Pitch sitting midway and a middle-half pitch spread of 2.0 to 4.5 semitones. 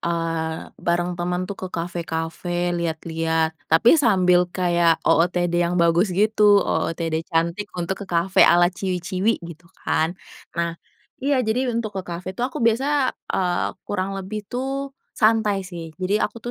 Yes: medium, 180 Hz; average, 3.4 semitones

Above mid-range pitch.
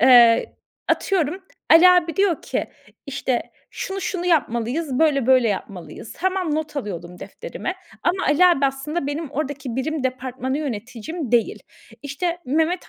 Yes: very high, 285 Hz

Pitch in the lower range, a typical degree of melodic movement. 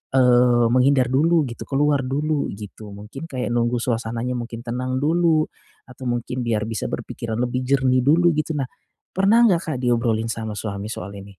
Yes: low, 125 Hz; average, 3.5 semitones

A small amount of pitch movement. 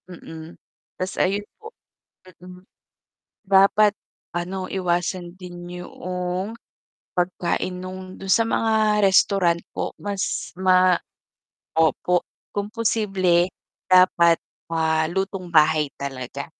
Yes: narrow, 2.0 semitones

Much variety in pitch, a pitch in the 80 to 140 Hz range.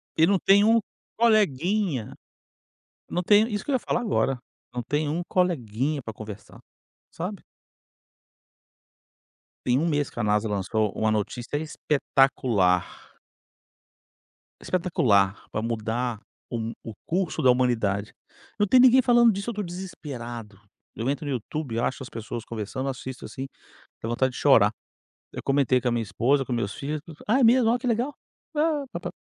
Yes: wide, 8.8 semitones; low, 135 Hz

